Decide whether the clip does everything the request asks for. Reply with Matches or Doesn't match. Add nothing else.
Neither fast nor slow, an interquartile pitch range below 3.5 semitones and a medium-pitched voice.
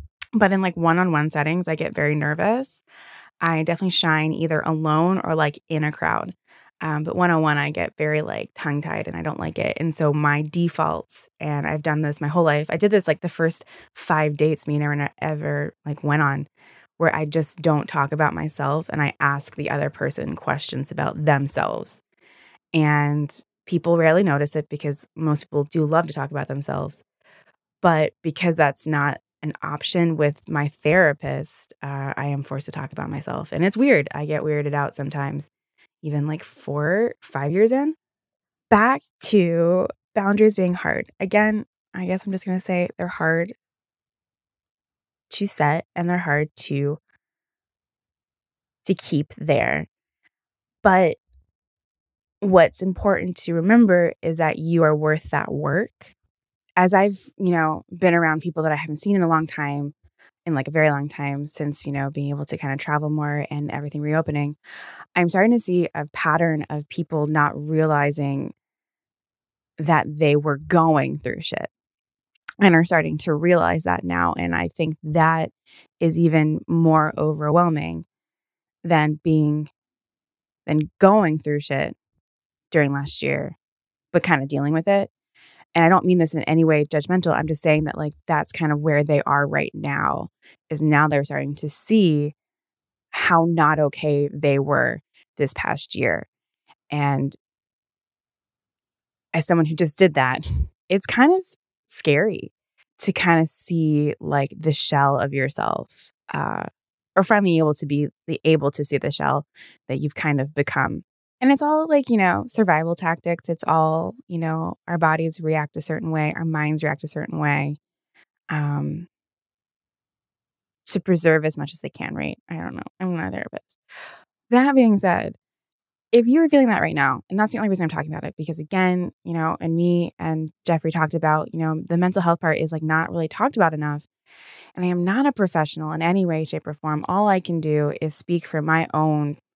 Matches